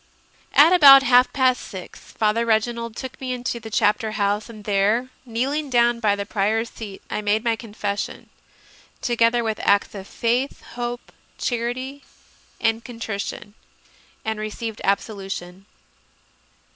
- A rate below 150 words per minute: Yes, average, 140 wpm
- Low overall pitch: No, high, 230 Hz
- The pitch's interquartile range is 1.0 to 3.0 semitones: Yes, average, 2.7 semitones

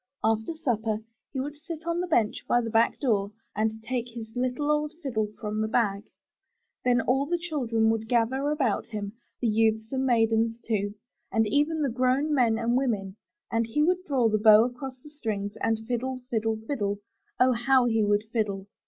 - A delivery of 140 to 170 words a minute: No, average, 190 wpm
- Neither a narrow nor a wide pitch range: Yes, average, 3.4 semitones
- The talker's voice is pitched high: Yes, high, 230 Hz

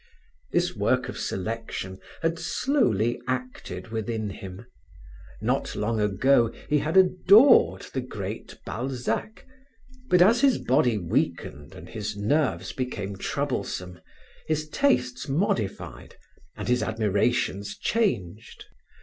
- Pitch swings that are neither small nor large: No, wide, 6.8 semitones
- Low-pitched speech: Yes, low, 120 Hz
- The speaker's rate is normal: No, slow, 110 wpm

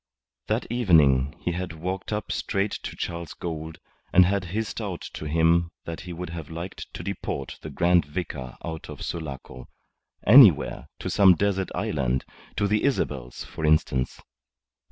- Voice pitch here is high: No, very low, 85 Hz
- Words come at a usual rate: Yes, average, 155 wpm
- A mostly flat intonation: No, average, 3.7 semitones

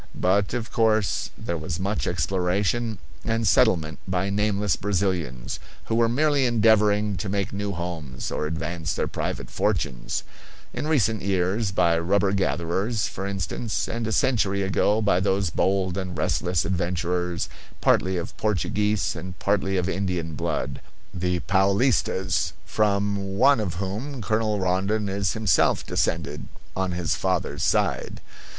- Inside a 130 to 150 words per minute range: Yes, average, 140 wpm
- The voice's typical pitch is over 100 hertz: No, very low, 95 Hz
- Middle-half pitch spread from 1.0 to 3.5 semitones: Yes, average, 3.0 semitones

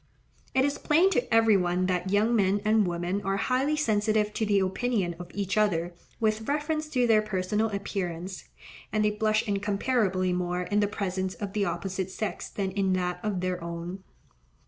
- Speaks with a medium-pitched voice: No, high, 200 Hz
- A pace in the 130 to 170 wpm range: No, average, 180 wpm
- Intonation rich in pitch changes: No, average, 2.9 semitones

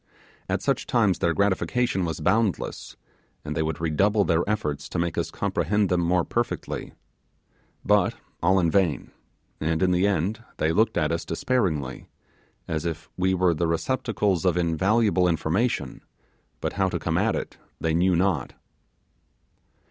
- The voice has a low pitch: Yes, very low, 90 Hz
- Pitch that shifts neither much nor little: Yes, average, 3.5 semitones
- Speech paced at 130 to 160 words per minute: Yes, average, 155 wpm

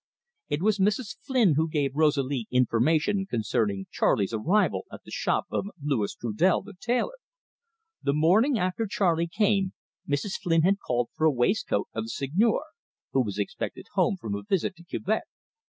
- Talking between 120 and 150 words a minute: No, average, 165 wpm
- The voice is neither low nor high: Yes, medium, 160 Hz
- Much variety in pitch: Yes, wide, 7.9 semitones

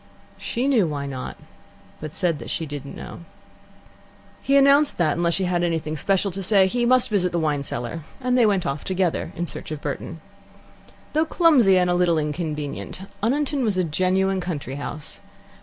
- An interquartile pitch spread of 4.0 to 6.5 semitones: Yes, wide, 5.6 semitones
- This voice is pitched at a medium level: Yes, medium, 180 Hz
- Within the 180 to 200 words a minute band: Yes, average, 190 wpm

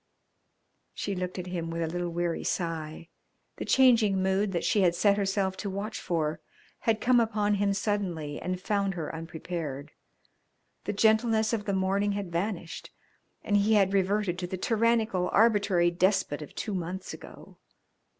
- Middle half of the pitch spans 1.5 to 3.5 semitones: Yes, average, 3.2 semitones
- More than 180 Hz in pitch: Yes, high, 190 Hz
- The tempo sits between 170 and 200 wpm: No, average, 160 wpm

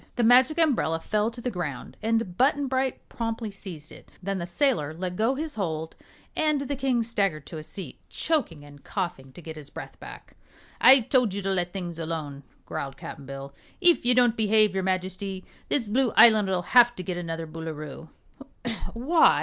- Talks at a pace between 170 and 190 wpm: Yes, average, 185 wpm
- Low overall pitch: No, high, 195 Hz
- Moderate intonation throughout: No, wide, 6.9 semitones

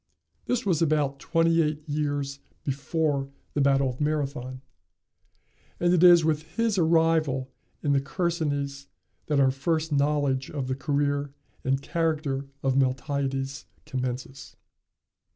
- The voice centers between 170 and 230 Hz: No, medium, 145 Hz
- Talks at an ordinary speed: No, slow, 125 wpm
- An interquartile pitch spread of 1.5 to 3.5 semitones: Yes, average, 2.7 semitones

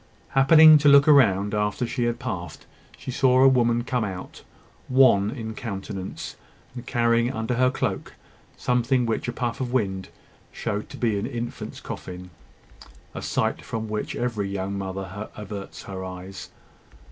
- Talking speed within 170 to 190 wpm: No, average, 155 wpm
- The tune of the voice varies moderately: Yes, average, 4.3 semitones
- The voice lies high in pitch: No, low, 115 Hz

